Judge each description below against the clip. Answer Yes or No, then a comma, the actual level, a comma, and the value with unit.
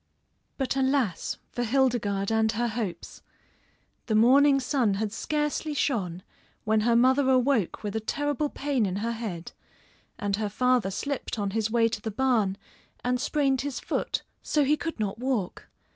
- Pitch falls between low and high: No, high, 235 Hz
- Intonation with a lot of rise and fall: No, average, 4.2 semitones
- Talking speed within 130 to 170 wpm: Yes, average, 160 wpm